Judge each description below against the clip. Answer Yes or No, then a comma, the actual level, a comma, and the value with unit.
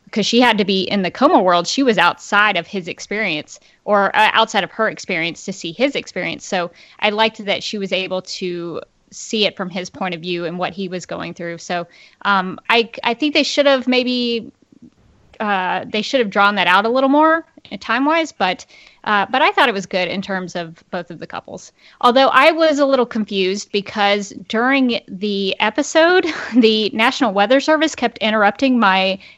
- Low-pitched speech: No, high, 210 Hz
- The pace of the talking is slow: No, fast, 205 wpm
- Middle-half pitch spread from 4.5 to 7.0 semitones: Yes, average, 5.0 semitones